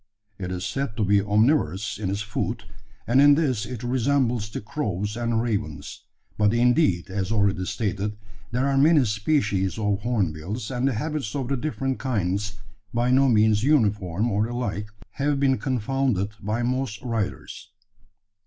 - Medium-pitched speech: No, low, 110 Hz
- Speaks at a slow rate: No, average, 155 wpm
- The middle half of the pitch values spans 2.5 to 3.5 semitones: No, average, 4.3 semitones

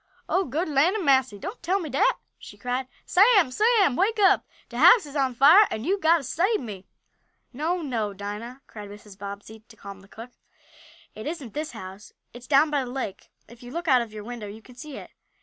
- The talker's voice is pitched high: Yes, very high, 260 Hz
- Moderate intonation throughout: No, wide, 7.4 semitones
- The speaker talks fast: Yes, fast, 215 wpm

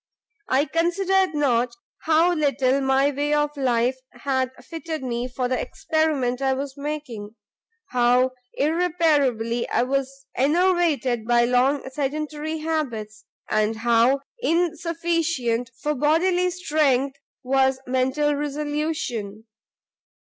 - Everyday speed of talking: No, slow, 105 wpm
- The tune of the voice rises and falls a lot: No, average, 3.9 semitones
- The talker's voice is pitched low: No, very high, 275 Hz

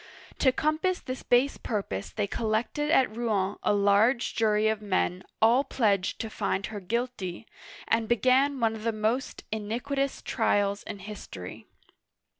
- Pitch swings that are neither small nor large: Yes, average, 3.8 semitones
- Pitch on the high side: Yes, high, 220 Hz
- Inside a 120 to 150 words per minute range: Yes, average, 145 wpm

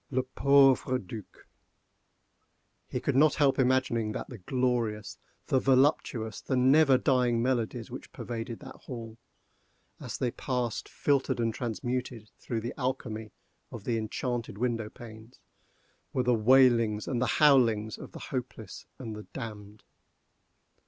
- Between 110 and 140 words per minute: Yes, slow, 135 wpm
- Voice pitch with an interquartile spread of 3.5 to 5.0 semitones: No, average, 2.7 semitones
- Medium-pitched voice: No, low, 120 Hz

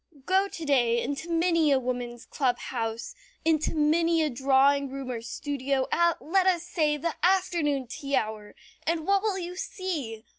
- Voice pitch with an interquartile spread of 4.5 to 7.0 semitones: Yes, average, 4.9 semitones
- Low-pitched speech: No, very high, 295 Hz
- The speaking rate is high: No, average, 170 wpm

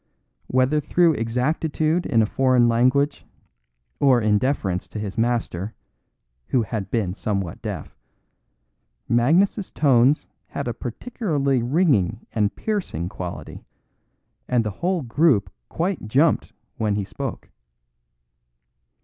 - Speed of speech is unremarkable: No, slow, 115 wpm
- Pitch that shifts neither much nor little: No, wide, 5.9 semitones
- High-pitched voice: No, low, 125 Hz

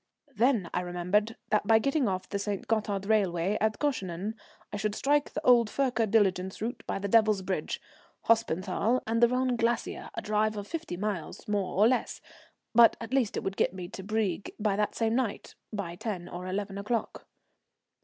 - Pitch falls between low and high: No, high, 210 Hz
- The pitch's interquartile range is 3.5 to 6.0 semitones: No, average, 3.0 semitones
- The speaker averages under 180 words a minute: No, average, 185 wpm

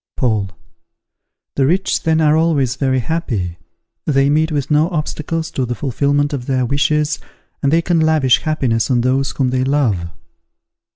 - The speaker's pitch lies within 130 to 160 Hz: Yes, medium, 140 Hz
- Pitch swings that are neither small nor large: Yes, average, 3.4 semitones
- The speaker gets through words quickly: No, average, 160 wpm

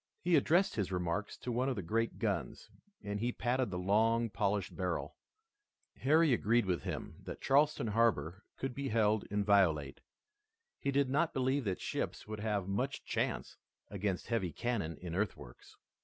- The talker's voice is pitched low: Yes, low, 110 Hz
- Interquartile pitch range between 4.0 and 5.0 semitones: Yes, average, 4.6 semitones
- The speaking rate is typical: Yes, average, 160 wpm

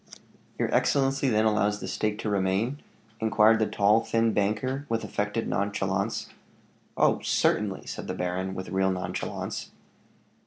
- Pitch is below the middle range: Yes, low, 105 Hz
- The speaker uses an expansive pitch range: No, average, 2.9 semitones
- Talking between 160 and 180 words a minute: No, average, 140 wpm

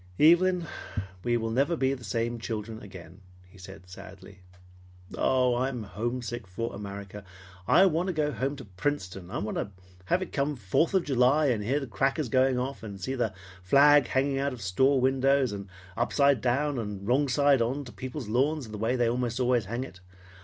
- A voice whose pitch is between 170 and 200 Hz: No, low, 125 Hz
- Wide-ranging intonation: No, average, 4.7 semitones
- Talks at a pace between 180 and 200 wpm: Yes, average, 190 wpm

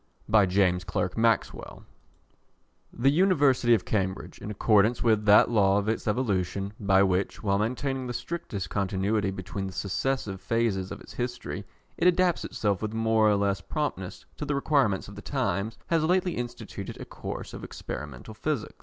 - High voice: No, low, 105 Hz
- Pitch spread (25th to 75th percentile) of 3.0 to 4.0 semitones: No, average, 4.6 semitones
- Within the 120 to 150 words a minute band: No, average, 165 wpm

